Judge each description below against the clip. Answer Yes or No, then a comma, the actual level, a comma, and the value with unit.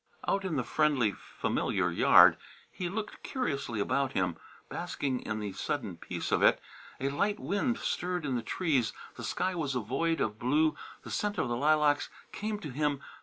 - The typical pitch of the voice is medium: Yes, medium, 145 Hz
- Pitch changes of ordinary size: No, wide, 6.2 semitones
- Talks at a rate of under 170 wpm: No, average, 180 wpm